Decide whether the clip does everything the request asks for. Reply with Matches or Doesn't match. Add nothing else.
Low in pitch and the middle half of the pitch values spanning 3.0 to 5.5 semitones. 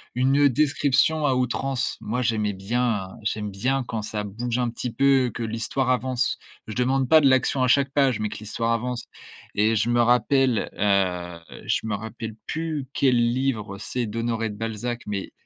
Matches